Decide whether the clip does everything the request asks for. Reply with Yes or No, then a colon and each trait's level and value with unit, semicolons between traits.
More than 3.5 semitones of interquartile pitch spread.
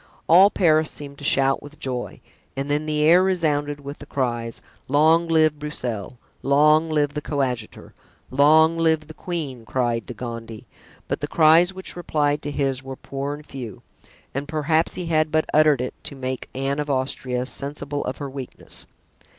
No: average, 2.8 semitones